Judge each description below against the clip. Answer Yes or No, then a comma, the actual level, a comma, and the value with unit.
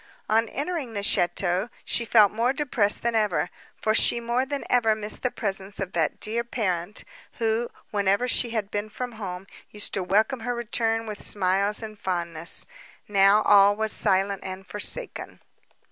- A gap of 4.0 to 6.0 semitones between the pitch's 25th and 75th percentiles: No, average, 3.1 semitones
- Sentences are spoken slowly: No, average, 165 wpm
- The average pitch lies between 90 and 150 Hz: No, high, 210 Hz